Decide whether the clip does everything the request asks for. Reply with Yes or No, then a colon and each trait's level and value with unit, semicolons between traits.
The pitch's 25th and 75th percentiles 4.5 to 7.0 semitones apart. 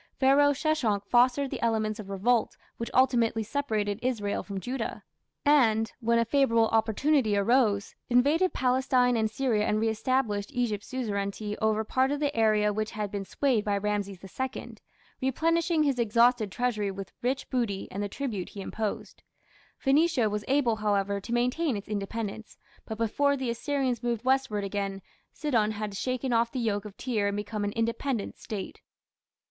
No: average, 3.8 semitones